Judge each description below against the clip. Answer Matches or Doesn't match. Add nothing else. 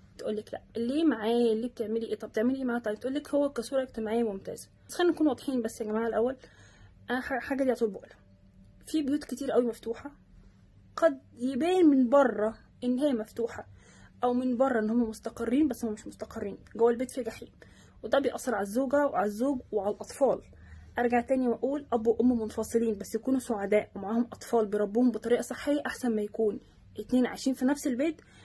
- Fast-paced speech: Matches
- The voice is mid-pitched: Doesn't match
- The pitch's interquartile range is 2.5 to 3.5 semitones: Matches